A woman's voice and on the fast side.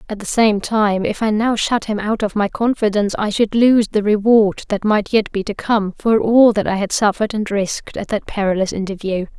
Yes: female; fast, 230 wpm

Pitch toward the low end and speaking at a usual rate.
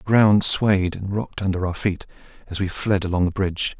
No: very low, 95 Hz; fast, 220 wpm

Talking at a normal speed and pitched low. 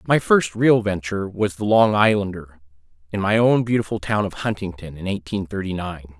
Yes: average, 185 wpm; low, 100 Hz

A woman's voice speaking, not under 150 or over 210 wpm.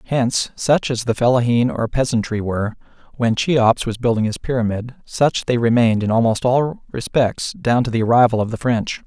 No: male; average, 185 wpm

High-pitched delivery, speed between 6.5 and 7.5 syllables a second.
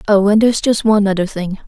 Yes: high, 205 Hz; 7.0 syllables/s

